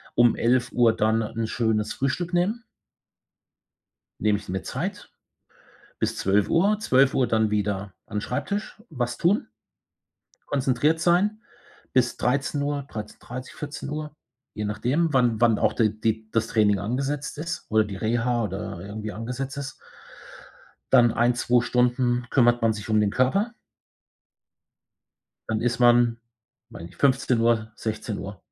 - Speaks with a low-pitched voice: Yes, low, 120 Hz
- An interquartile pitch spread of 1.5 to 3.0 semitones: No, average, 4.1 semitones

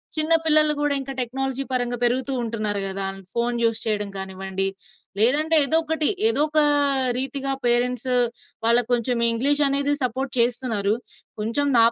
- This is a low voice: No, very high, 250 Hz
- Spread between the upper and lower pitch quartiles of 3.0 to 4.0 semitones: Yes, average, 3.7 semitones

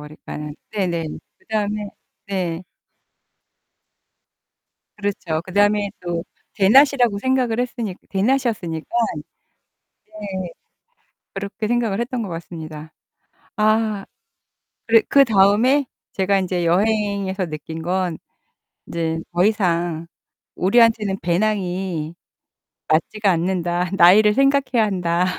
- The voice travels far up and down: No, average, 3.9 semitones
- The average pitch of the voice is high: Yes, high, 195 Hz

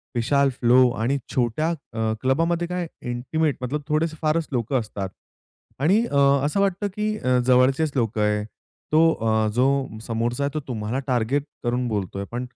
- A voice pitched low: Yes, low, 130 Hz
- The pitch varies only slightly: No, average, 4.8 semitones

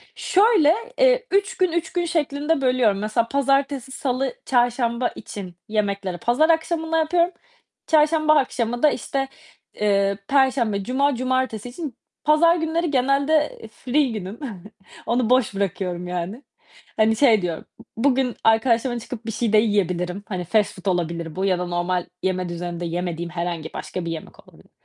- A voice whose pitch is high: Yes, high, 240 Hz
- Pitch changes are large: Yes, wide, 6.7 semitones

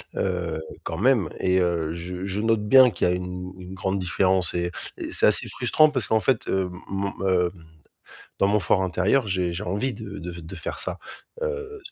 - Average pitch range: Yes, average, 3.1 semitones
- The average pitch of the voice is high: No, very low, 95 Hz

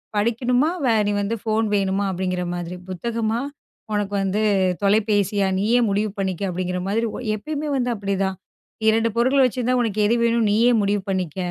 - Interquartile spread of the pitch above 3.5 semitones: No, average, 3.1 semitones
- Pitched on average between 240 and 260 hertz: No, high, 210 Hz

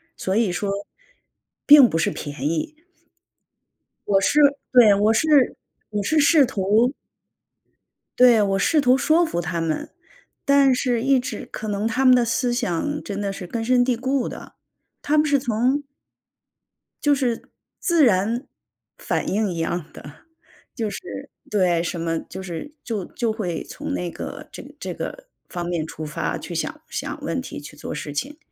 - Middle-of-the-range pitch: No, high, 225 Hz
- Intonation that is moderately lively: No, wide, 6.3 semitones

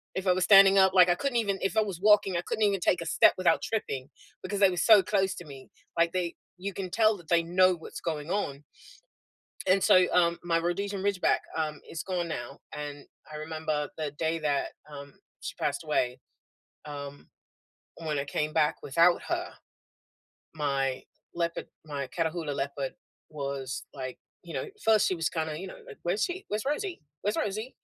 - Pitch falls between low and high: Yes, medium, 170 Hz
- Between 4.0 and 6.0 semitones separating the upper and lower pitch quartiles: Yes, average, 4.6 semitones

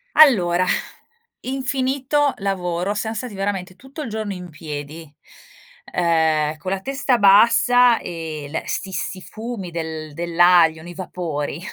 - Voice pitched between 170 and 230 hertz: Yes, medium, 185 Hz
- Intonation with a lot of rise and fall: Yes, wide, 5.9 semitones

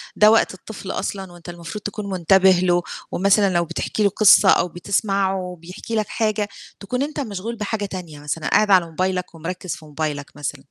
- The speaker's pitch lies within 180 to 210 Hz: Yes, high, 190 Hz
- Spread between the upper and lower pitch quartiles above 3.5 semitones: No, average, 3.1 semitones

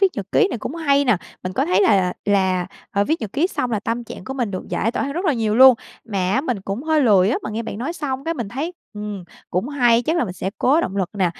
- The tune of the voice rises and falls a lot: Yes, wide, 5.9 semitones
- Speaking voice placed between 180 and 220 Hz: No, high, 235 Hz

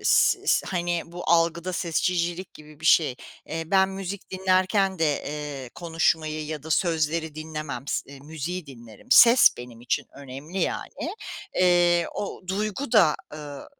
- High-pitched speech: No, medium, 165 Hz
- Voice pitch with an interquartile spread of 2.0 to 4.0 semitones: Yes, average, 3.5 semitones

